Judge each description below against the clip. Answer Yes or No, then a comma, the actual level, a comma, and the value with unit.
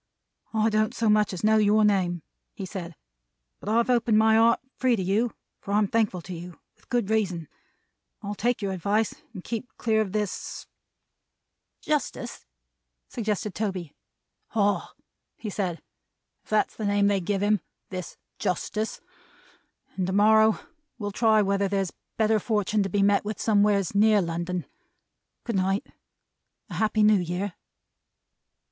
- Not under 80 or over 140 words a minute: No, average, 150 wpm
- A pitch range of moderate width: No, narrow, 2.2 semitones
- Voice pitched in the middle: No, high, 205 Hz